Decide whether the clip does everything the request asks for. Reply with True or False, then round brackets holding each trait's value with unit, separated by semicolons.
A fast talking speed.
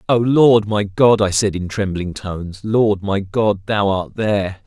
False (195 wpm)